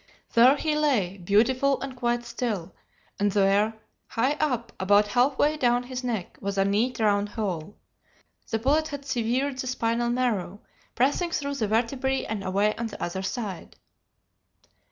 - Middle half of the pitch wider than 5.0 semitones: No, average, 4.3 semitones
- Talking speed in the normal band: Yes, average, 155 wpm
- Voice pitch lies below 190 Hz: No, high, 235 Hz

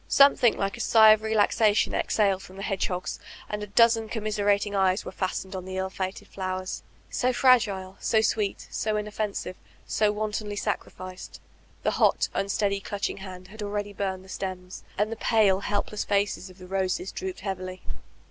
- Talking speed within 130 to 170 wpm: No, average, 180 wpm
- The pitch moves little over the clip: Yes, narrow, 2.3 semitones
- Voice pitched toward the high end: Yes, high, 200 Hz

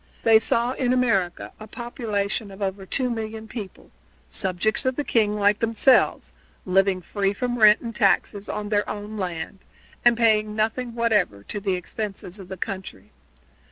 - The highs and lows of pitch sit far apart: No, average, 2.8 semitones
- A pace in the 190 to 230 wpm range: No, average, 160 wpm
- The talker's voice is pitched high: Yes, high, 210 Hz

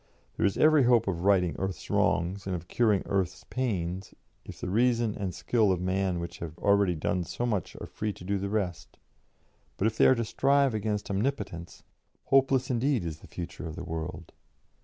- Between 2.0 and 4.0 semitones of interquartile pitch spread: No, average, 4.6 semitones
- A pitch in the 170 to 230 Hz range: No, low, 100 Hz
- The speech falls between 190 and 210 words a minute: Yes, average, 195 wpm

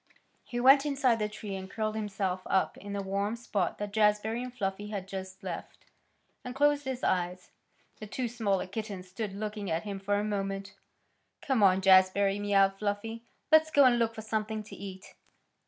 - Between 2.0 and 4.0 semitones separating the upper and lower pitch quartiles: Yes, average, 2.7 semitones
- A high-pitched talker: Yes, high, 205 Hz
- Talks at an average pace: Yes, average, 185 wpm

